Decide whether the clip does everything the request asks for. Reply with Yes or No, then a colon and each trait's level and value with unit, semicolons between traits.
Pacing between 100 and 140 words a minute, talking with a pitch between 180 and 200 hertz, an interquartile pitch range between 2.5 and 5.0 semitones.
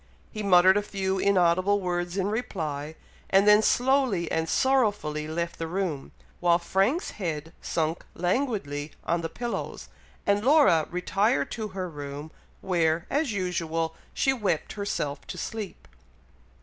Yes: slow, 135 wpm; medium, 185 Hz; average, 4.2 semitones